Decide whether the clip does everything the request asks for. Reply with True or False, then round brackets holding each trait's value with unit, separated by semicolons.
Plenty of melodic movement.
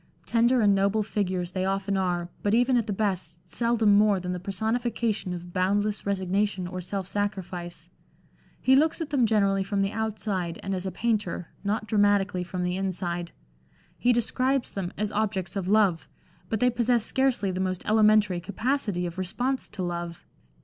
False (3.1 semitones)